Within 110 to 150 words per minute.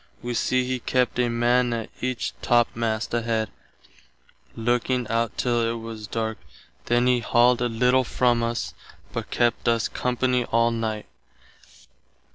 Yes: average, 140 wpm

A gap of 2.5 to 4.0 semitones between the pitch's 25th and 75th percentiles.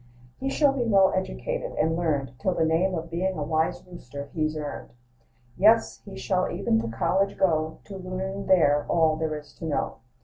Yes: average, 3.7 semitones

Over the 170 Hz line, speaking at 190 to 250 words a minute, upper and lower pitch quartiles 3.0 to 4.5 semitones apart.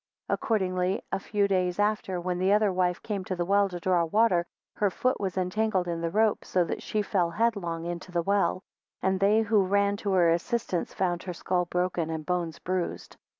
No: medium, 185 Hz; fast, 205 wpm; narrow, 2.5 semitones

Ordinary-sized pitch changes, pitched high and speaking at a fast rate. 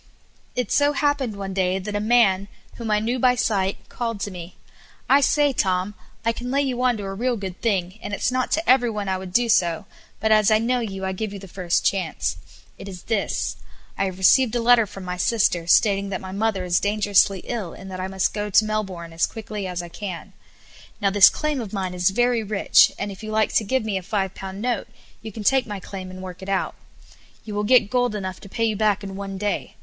Yes: average, 3.3 semitones; high, 205 Hz; fast, 245 wpm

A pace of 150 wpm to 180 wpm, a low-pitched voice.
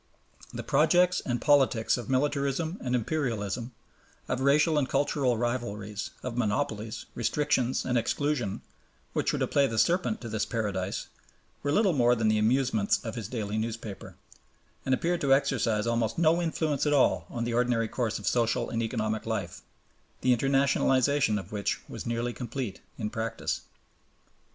Yes: average, 155 wpm; low, 120 Hz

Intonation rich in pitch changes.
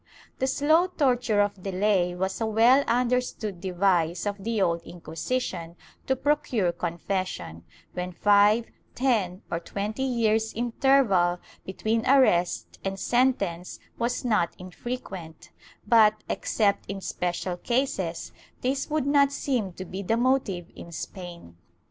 Yes: wide, 5.7 semitones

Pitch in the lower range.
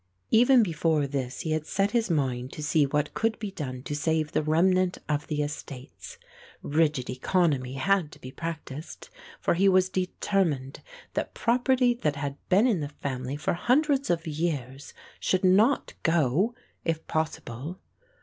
No: medium, 160 Hz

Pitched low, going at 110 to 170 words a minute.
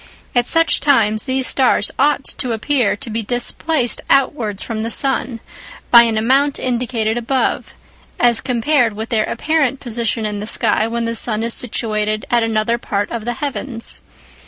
No: high, 235 Hz; average, 165 wpm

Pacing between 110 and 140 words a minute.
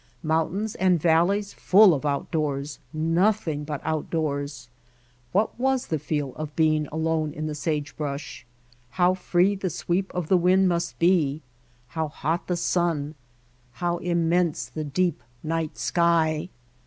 Yes: slow, 135 wpm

